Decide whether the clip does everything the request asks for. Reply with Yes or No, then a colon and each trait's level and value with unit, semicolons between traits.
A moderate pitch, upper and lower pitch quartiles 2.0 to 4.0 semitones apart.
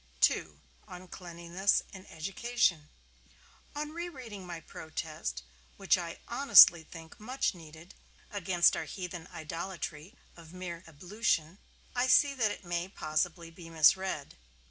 Yes: medium, 175 Hz; average, 3.6 semitones